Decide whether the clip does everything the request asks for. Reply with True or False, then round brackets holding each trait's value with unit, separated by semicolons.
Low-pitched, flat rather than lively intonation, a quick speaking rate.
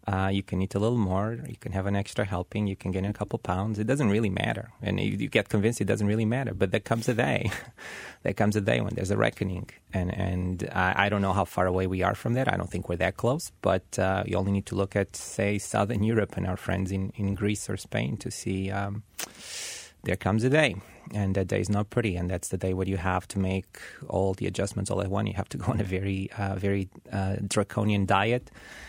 True (100 Hz; 2.3 semitones; 255 wpm)